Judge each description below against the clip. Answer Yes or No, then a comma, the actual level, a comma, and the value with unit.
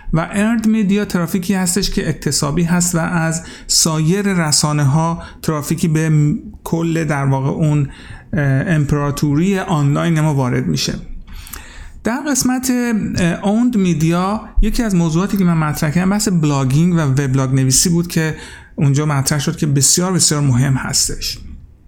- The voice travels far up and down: No, average, 4.2 semitones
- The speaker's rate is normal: Yes, average, 135 wpm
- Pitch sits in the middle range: Yes, medium, 165 Hz